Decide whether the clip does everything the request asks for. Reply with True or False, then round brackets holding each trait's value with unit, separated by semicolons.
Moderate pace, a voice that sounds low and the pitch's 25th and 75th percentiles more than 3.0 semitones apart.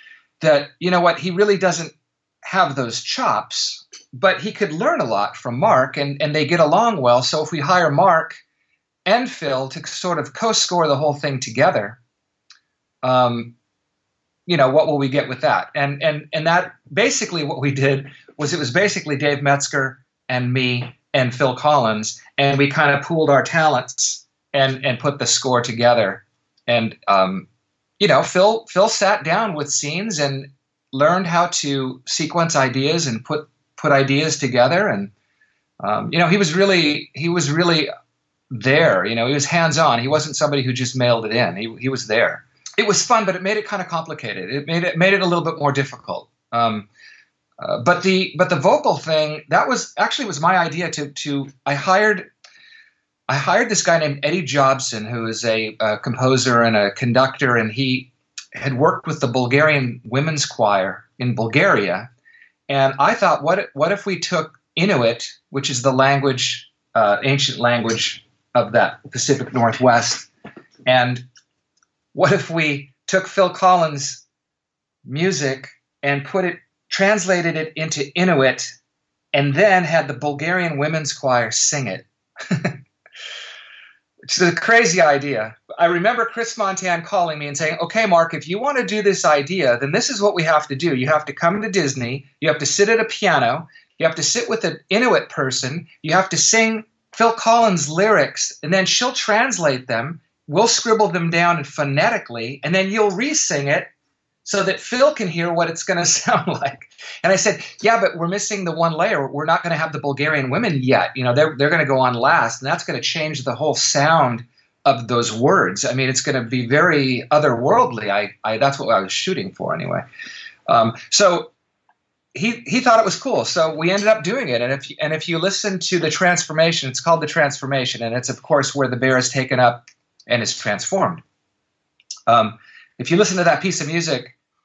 False (190 wpm; 155 Hz; 5.2 semitones)